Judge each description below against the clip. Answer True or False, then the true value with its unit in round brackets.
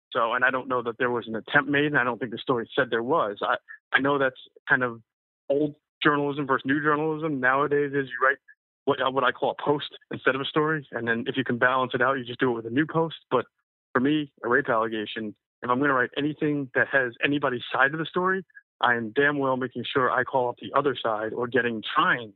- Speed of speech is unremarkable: False (255 wpm)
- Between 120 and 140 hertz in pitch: True (135 Hz)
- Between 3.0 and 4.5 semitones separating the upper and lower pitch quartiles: True (3.4 semitones)